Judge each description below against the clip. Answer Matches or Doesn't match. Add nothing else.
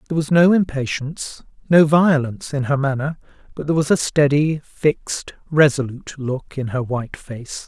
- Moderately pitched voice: Matches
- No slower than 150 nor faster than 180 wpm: Matches